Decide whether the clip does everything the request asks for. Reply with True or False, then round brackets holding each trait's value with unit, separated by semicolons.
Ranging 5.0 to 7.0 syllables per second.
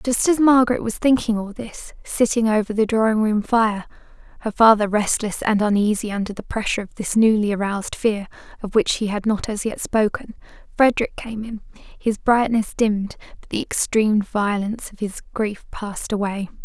True (5.3 syllables/s)